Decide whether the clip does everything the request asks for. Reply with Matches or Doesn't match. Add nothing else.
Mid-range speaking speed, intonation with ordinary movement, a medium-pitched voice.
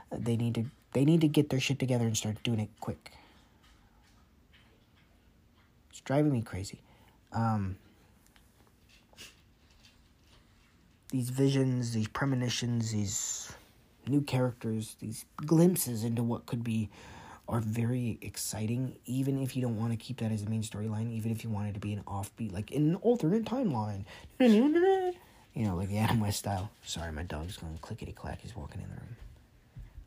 Doesn't match